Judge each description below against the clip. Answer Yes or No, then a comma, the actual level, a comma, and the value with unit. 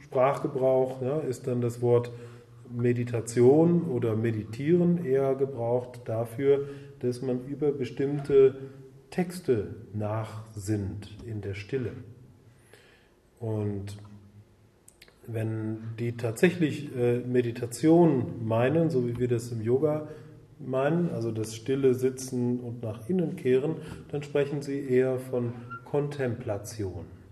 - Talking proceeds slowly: Yes, slow, 110 wpm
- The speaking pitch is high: No, low, 125 Hz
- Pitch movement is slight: No, average, 3.3 semitones